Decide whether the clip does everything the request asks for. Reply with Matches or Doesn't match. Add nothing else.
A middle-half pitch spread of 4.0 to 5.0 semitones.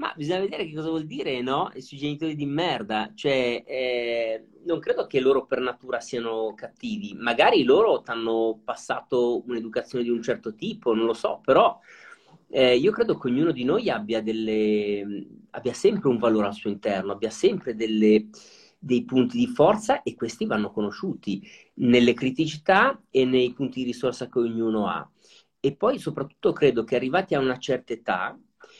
Matches